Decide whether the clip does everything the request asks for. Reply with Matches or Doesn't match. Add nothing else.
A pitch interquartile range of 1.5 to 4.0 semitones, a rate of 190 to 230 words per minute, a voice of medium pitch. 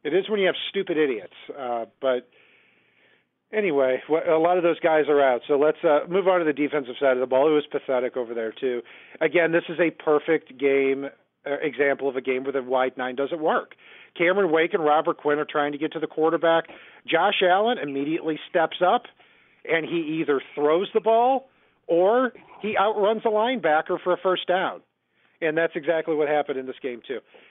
Doesn't match